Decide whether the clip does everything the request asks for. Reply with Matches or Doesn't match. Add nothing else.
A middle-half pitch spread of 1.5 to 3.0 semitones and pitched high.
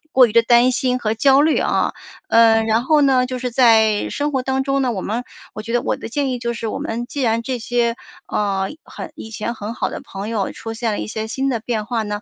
Matches